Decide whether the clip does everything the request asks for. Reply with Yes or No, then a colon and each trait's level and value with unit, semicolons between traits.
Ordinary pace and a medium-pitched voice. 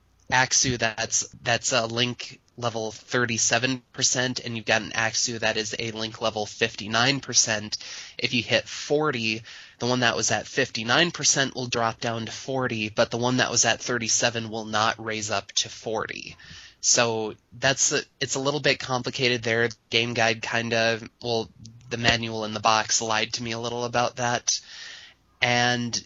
No: average, 170 wpm; low, 115 Hz